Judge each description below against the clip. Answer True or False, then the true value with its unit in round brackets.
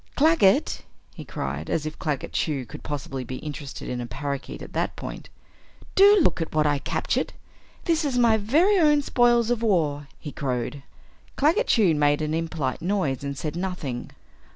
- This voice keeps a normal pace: True (175 wpm)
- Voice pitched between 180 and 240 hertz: False (155 Hz)